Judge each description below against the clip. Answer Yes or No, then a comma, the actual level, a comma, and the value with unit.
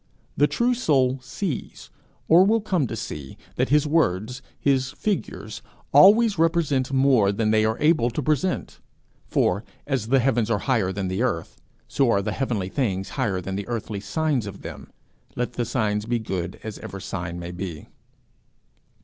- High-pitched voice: No, low, 120 Hz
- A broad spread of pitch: Yes, wide, 6.3 semitones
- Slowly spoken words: No, average, 170 wpm